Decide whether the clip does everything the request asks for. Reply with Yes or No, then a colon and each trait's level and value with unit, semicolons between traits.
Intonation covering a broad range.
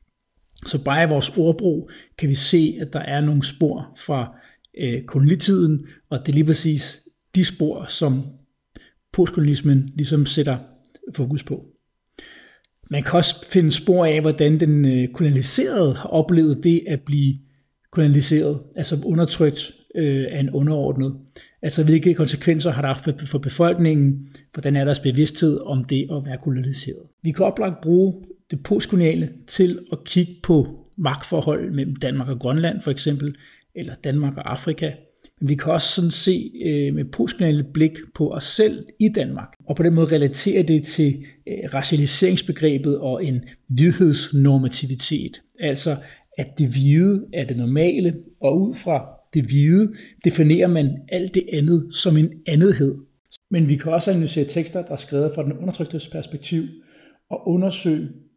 No: average, 3.2 semitones